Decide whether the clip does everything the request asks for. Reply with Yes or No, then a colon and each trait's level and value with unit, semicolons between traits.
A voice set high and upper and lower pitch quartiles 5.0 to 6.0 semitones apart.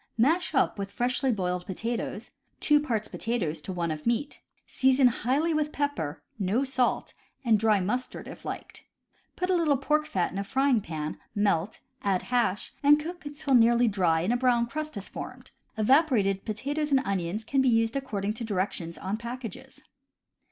Yes: high, 235 Hz; wide, 5.6 semitones